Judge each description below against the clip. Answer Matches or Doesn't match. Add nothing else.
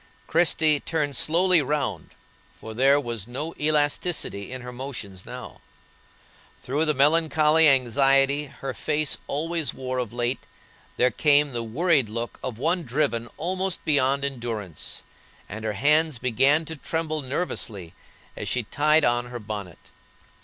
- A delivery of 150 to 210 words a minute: Doesn't match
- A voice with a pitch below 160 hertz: Matches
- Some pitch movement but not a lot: Matches